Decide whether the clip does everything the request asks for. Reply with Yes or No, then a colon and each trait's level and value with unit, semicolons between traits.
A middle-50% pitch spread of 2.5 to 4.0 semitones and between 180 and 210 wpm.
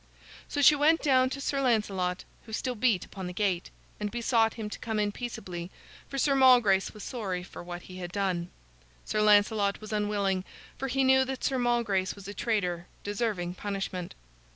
No: average, 4.6 semitones; average, 185 wpm